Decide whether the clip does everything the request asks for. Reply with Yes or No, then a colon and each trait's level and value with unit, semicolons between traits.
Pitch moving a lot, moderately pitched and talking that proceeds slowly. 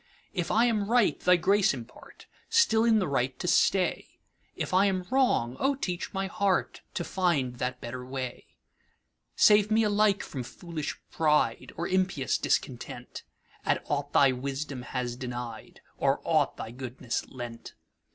Yes: wide, 7.8 semitones; medium, 160 Hz; slow, 130 wpm